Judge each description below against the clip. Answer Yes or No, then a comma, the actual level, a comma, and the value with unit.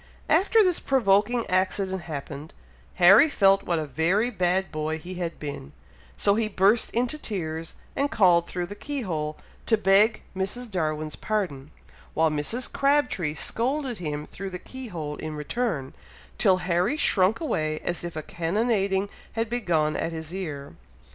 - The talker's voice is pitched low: No, medium, 185 Hz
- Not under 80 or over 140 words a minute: No, average, 155 wpm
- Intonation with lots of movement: Yes, wide, 6.0 semitones